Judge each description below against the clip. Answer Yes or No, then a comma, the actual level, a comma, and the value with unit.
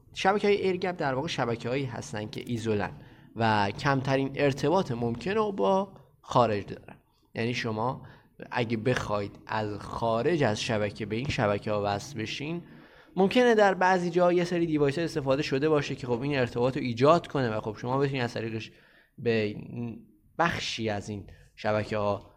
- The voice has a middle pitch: No, low, 125 Hz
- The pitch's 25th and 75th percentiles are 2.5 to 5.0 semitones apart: No, wide, 5.5 semitones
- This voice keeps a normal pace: No, fast, 160 wpm